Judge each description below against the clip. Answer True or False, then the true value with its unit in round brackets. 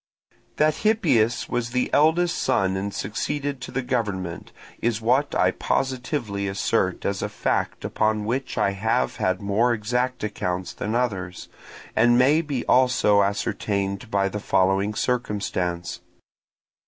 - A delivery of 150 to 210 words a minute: False (135 wpm)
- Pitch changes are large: False (4.3 semitones)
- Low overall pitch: True (110 Hz)